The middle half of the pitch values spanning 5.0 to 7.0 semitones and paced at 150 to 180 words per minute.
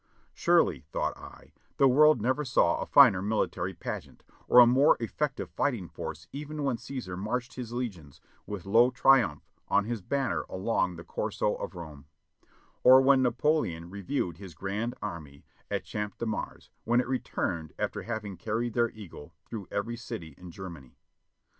Yes: wide, 5.6 semitones; average, 160 wpm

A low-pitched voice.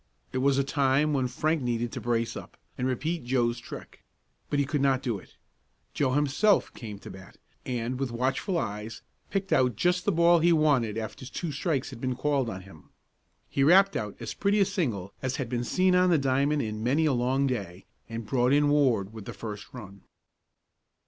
Yes: low, 130 Hz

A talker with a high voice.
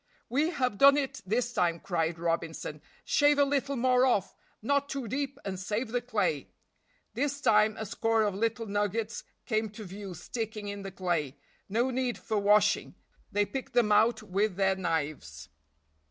Yes: high, 215 Hz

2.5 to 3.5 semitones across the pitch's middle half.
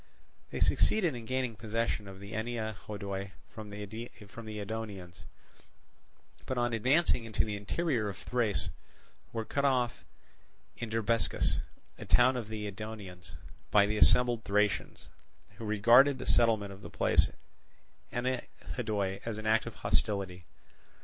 Yes: average, 2.8 semitones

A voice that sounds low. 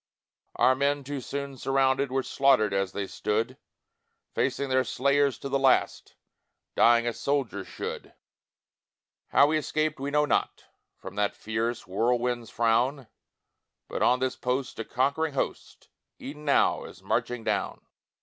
Yes: low, 130 Hz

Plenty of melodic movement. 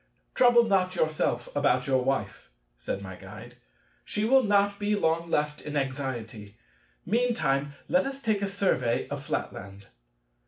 Yes: wide, 9.0 semitones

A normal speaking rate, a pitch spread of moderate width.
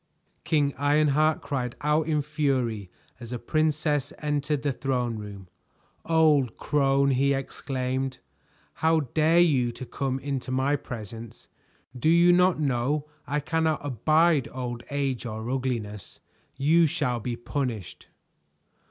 No: slow, 125 wpm; average, 3.5 semitones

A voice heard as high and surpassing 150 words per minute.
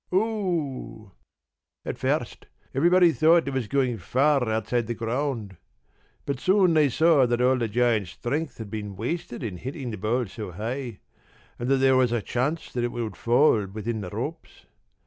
No: low, 125 Hz; average, 175 wpm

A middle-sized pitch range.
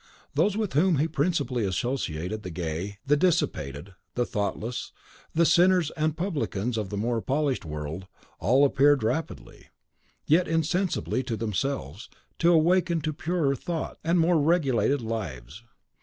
No: wide, 8.0 semitones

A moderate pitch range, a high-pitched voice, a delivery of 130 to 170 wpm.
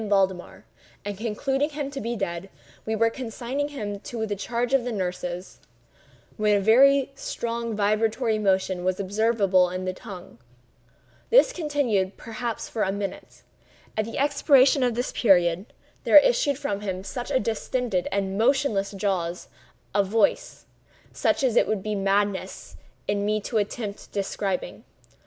Yes: average, 4.0 semitones; high, 215 Hz; average, 140 wpm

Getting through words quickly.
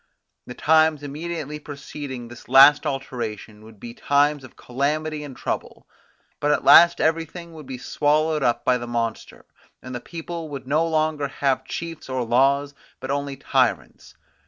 No: average, 160 wpm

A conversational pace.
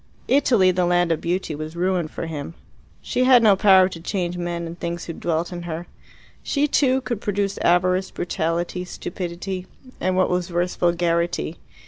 Yes: average, 170 wpm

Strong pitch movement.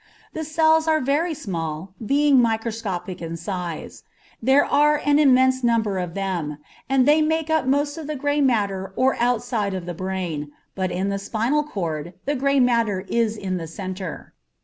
Yes: wide, 7.3 semitones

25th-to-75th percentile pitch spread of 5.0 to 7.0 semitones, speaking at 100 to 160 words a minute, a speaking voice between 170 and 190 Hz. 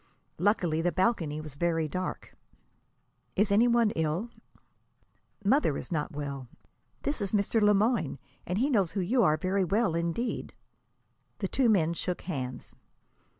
Yes: average, 5.3 semitones; average, 150 wpm; medium, 185 Hz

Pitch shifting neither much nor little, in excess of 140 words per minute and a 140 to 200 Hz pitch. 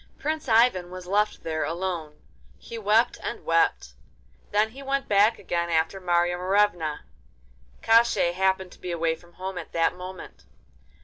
Yes: average, 3.6 semitones; average, 150 wpm; medium, 185 Hz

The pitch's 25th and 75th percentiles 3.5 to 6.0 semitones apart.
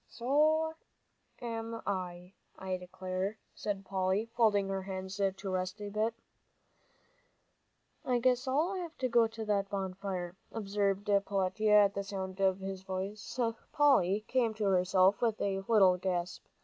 No: average, 3.0 semitones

